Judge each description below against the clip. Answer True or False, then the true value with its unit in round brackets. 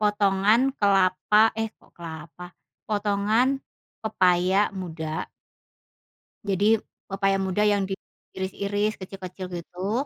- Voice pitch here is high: True (195 Hz)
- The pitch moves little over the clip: True (2.3 semitones)